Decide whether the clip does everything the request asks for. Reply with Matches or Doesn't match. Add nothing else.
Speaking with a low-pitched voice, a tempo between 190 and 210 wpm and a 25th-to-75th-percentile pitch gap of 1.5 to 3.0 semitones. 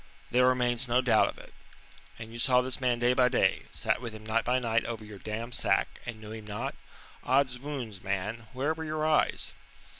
Matches